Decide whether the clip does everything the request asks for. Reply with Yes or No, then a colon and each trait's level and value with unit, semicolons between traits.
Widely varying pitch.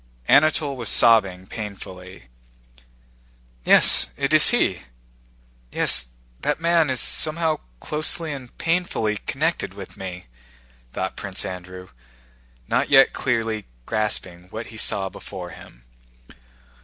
Yes: wide, 8.4 semitones